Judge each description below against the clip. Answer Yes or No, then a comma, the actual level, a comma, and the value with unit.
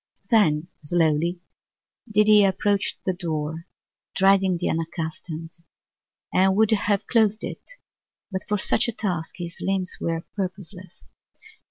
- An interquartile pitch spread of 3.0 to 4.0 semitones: Yes, average, 3.6 semitones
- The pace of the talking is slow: Yes, slow, 125 wpm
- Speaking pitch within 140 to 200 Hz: Yes, medium, 185 Hz